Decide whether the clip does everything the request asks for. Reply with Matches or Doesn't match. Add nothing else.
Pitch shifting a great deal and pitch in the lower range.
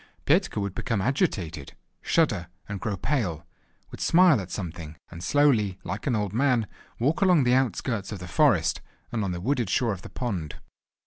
Matches